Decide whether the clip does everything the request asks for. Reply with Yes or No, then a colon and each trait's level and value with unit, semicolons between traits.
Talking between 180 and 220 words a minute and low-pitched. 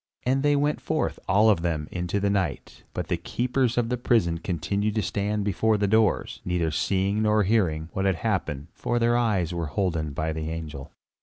Yes: average, 200 wpm; low, 100 Hz